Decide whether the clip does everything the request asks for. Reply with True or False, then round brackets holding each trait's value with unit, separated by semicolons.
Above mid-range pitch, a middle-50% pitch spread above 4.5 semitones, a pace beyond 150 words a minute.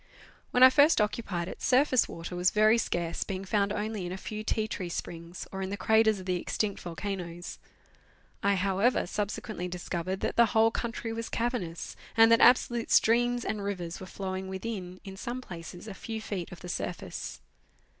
False (200 Hz; 3.9 semitones; 185 wpm)